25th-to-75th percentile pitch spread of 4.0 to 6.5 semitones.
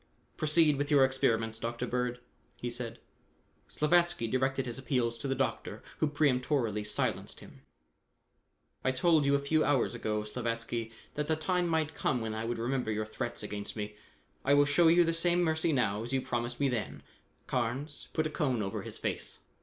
Yes: average, 4.4 semitones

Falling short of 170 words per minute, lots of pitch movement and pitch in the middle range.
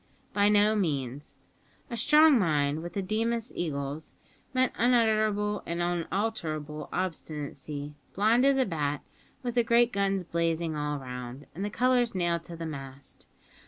Yes: average, 145 wpm; wide, 6.7 semitones; medium, 175 Hz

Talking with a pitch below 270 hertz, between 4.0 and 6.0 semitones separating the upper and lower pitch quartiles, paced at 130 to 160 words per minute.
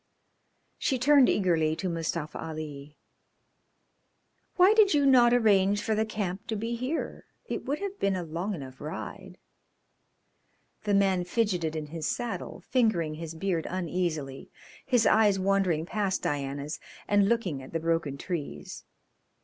Yes: medium, 185 Hz; wide, 5.6 semitones; average, 140 wpm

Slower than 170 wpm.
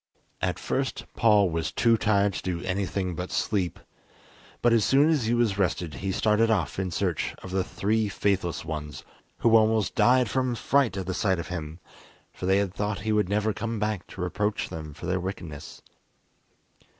No: average, 185 wpm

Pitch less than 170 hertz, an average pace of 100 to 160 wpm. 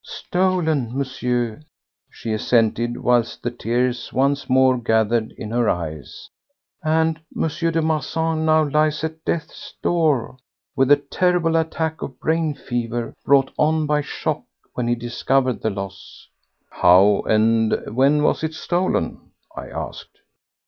Yes: low, 135 Hz; slow, 135 wpm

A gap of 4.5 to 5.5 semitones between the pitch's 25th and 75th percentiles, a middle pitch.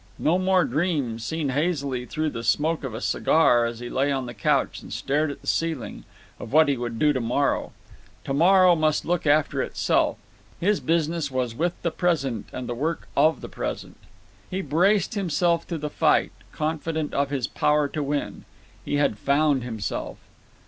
No: average, 4.1 semitones; medium, 150 Hz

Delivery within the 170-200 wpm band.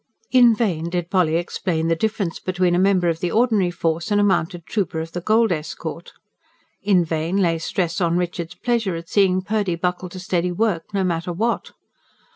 Yes: average, 190 wpm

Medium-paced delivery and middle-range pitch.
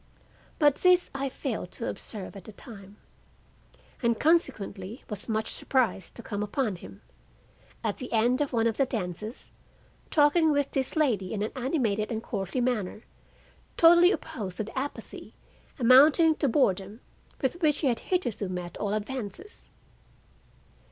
No: average, 150 wpm; high, 235 Hz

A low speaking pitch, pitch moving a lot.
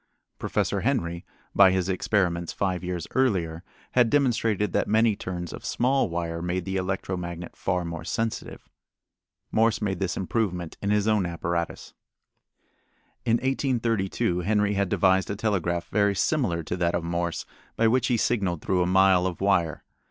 No: very low, 95 Hz; average, 3.8 semitones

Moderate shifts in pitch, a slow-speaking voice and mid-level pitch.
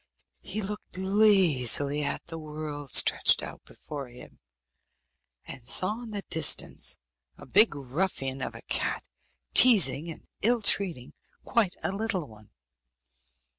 No: wide, 6.4 semitones; slow, 130 wpm; medium, 165 Hz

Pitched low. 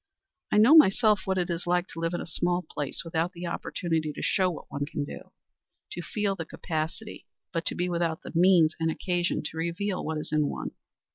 No: medium, 170 Hz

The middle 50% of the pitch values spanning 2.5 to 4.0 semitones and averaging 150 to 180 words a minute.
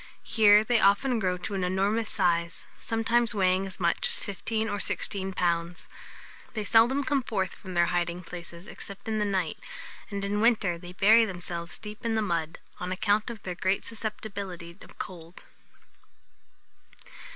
Yes: average, 3.5 semitones; average, 160 wpm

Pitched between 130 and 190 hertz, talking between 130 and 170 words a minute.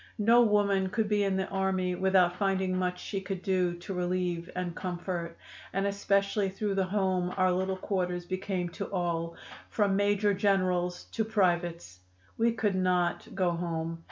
Yes: medium, 185 Hz; average, 160 wpm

